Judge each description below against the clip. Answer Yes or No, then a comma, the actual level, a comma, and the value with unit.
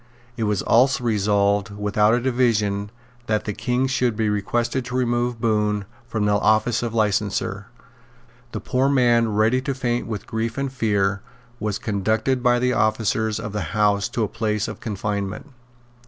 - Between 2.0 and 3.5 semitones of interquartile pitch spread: Yes, average, 2.8 semitones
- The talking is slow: No, average, 165 wpm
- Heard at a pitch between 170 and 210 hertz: No, low, 110 Hz